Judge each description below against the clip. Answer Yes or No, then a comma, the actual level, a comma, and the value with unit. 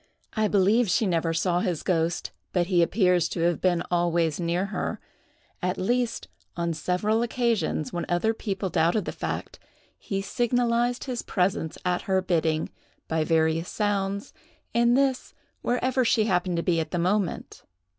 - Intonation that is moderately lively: Yes, average, 4.4 semitones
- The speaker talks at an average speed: Yes, average, 155 wpm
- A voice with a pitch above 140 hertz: Yes, medium, 185 Hz